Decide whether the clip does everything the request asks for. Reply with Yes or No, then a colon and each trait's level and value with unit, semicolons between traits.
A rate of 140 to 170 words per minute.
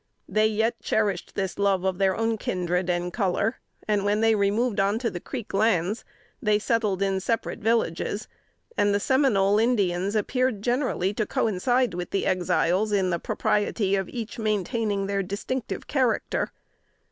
Yes: average, 160 wpm